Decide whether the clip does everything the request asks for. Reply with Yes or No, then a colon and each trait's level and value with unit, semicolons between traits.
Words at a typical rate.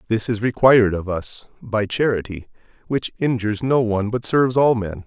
Yes: average, 180 wpm